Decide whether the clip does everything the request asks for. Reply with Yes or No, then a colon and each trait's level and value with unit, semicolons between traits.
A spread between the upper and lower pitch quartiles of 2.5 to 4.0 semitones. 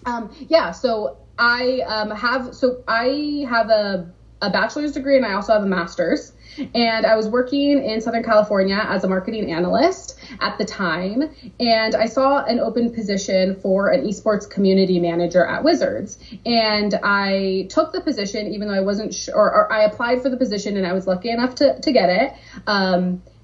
No: average, 4.6 semitones